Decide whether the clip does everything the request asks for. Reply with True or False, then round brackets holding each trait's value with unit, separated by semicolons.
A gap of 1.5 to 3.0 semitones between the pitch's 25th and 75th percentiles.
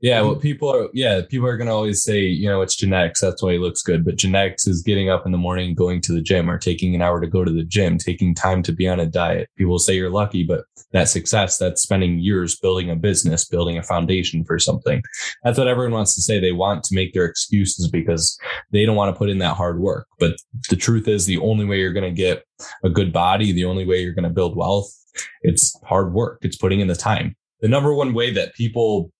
True (2.7 semitones)